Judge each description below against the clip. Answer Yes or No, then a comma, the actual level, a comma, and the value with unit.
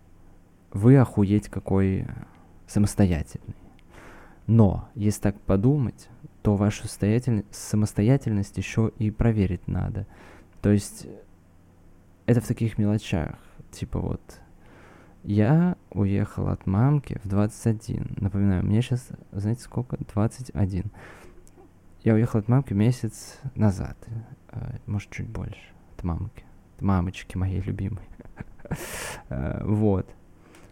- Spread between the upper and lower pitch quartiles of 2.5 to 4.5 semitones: Yes, average, 3.7 semitones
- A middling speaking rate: No, slow, 100 wpm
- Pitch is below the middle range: Yes, low, 105 Hz